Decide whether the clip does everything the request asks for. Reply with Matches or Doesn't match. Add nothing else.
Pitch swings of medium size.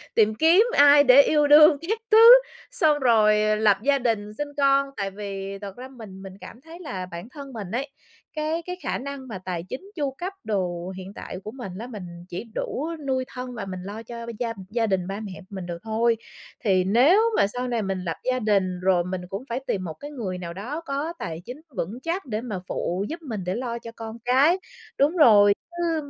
Doesn't match